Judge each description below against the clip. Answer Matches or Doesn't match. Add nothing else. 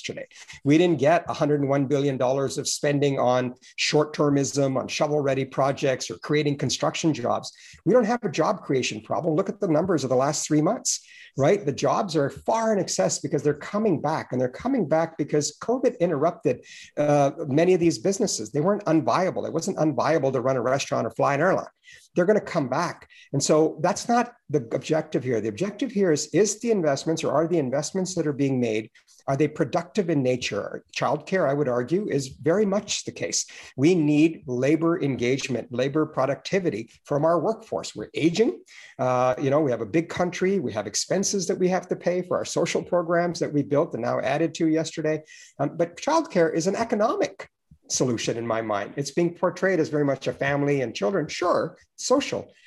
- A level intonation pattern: Doesn't match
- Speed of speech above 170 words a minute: Matches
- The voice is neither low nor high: Matches